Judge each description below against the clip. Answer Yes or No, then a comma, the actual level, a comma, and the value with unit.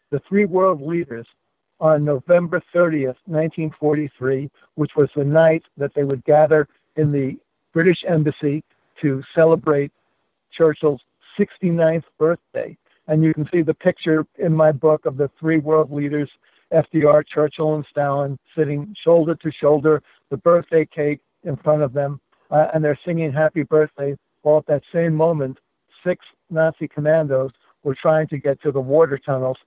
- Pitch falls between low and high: Yes, medium, 155 Hz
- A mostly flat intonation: Yes, narrow, 2.0 semitones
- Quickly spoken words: No, average, 155 wpm